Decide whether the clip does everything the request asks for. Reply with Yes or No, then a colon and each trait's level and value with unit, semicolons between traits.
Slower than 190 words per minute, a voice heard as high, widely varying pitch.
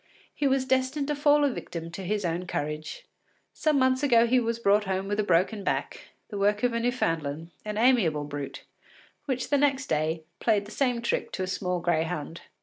No: average, 200 wpm; high, 210 Hz; wide, 7.3 semitones